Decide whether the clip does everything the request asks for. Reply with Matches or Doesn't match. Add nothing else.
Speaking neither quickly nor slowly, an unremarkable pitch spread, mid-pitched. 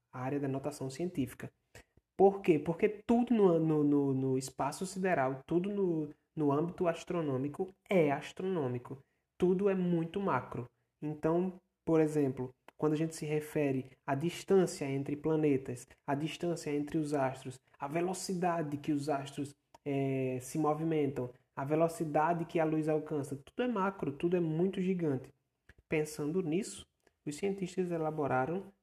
Matches